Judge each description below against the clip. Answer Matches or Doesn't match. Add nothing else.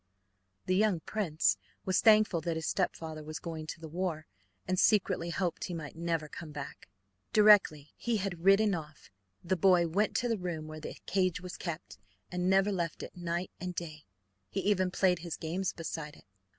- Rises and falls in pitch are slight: Doesn't match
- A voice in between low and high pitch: Matches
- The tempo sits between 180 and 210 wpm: Matches